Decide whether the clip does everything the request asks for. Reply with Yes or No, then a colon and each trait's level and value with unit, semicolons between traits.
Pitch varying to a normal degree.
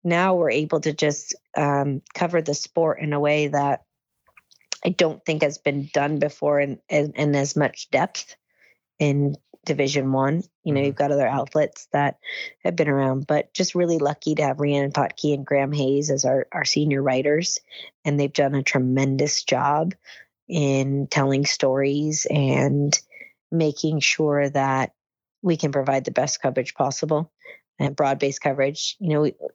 No: narrow, 1.9 semitones